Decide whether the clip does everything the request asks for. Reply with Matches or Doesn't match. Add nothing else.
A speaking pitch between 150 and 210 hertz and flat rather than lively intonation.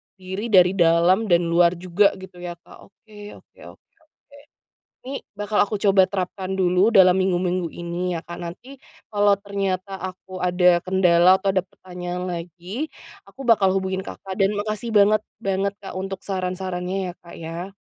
Matches